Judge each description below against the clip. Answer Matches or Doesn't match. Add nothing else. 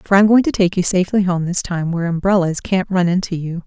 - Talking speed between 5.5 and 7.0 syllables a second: Matches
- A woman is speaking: Matches